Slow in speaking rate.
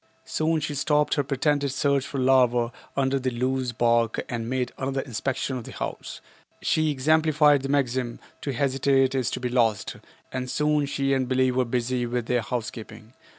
No: average, 175 wpm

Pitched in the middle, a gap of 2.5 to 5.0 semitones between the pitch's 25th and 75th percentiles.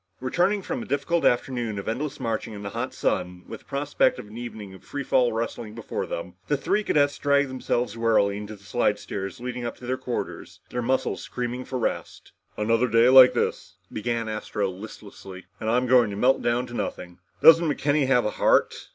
No: low, 120 Hz; average, 3.6 semitones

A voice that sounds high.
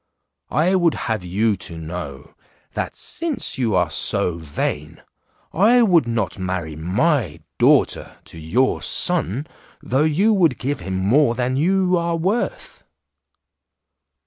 No: low, 125 Hz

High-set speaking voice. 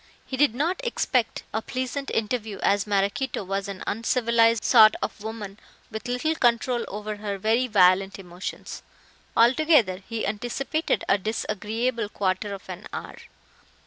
Yes: high, 220 Hz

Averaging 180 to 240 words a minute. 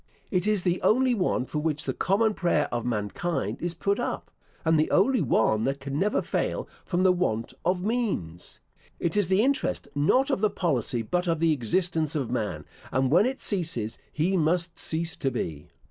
Yes: average, 190 wpm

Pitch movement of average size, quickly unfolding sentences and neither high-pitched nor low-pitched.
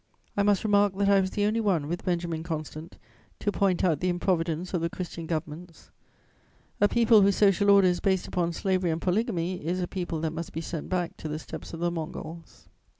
Yes: average, 3.1 semitones; fast, 210 wpm; medium, 180 Hz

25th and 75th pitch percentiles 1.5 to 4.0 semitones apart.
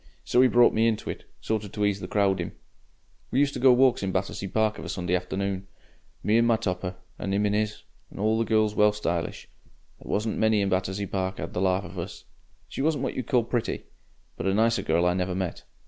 Yes: average, 3.0 semitones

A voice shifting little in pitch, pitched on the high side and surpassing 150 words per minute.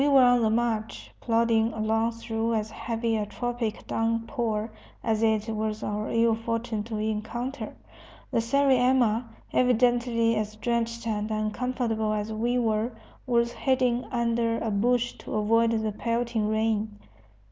No: narrow, 1.6 semitones; high, 230 Hz; average, 140 wpm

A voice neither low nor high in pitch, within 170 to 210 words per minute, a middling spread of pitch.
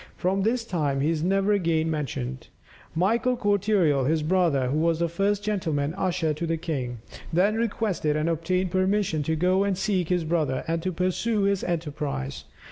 Yes: medium, 170 Hz; average, 180 wpm; average, 4.2 semitones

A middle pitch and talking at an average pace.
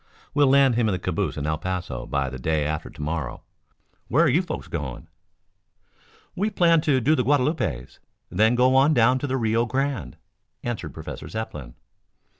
No: low, 120 Hz; average, 180 wpm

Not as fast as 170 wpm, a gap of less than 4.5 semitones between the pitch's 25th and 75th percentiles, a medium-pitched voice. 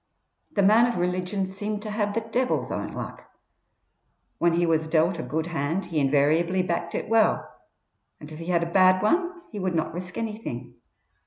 No: average, 185 wpm; average, 4.1 semitones; medium, 180 Hz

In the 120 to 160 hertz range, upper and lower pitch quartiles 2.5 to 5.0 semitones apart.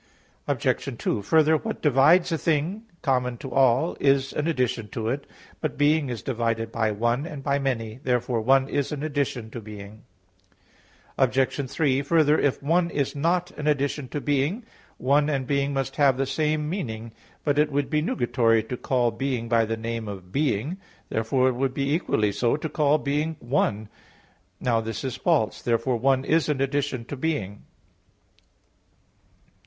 Yes: low, 135 Hz; average, 4.1 semitones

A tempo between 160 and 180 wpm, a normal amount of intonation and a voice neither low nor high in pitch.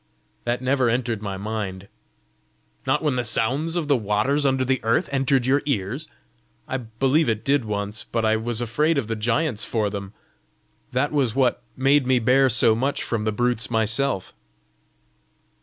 No: average, 170 wpm; average, 3.7 semitones; low, 120 Hz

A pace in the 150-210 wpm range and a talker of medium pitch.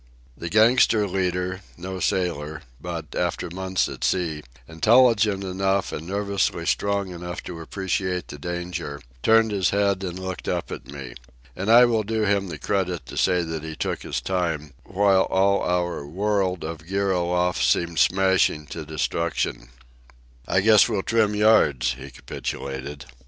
No: average, 155 wpm; very low, 90 Hz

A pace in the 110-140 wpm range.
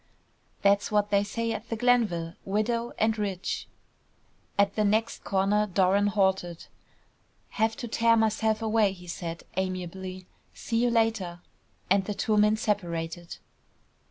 Yes: slow, 135 wpm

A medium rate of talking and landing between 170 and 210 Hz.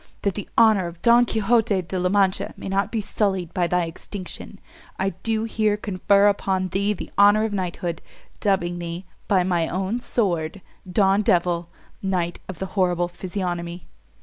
Yes: average, 165 wpm; high, 190 Hz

